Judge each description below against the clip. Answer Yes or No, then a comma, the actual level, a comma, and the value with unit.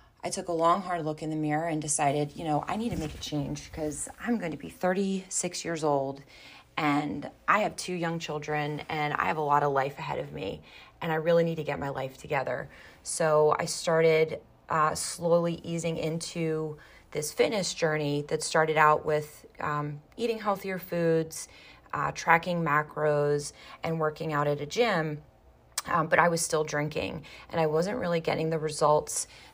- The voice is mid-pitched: Yes, medium, 155 Hz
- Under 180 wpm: No, average, 185 wpm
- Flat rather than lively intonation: Yes, narrow, 2.1 semitones